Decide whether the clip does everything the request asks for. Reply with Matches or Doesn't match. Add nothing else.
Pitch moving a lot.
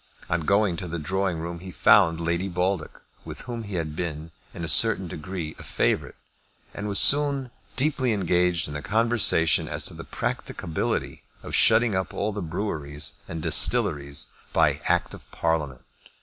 Doesn't match